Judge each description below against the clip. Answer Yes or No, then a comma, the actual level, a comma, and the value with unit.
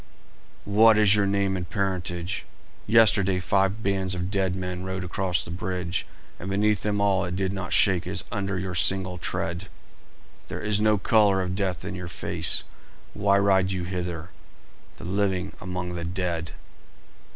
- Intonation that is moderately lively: No, narrow, 1.7 semitones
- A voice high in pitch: No, very low, 95 Hz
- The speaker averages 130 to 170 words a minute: Yes, average, 160 wpm